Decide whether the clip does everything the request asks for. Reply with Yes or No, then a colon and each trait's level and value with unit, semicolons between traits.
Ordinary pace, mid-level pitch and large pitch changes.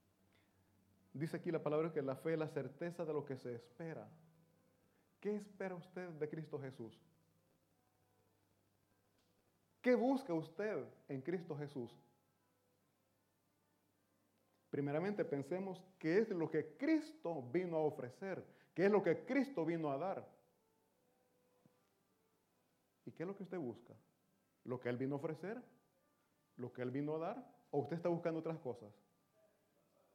Yes: average, 140 wpm; medium, 155 Hz; wide, 6.6 semitones